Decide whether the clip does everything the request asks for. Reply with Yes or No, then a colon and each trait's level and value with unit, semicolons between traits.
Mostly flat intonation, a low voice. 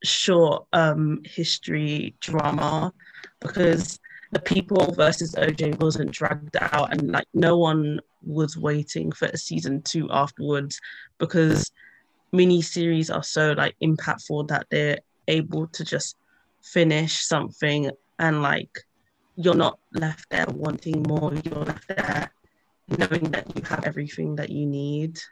No: narrow, 2.2 semitones; medium, 155 Hz